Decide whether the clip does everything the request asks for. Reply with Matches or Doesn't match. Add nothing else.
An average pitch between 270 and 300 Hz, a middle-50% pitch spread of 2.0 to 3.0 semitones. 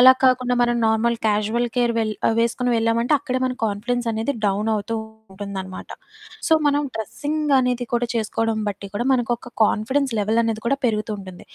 Doesn't match